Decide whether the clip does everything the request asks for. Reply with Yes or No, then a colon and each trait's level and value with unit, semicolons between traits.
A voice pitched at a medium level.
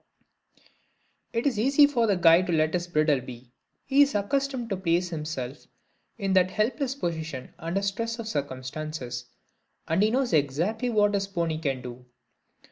Yes: medium, 180 Hz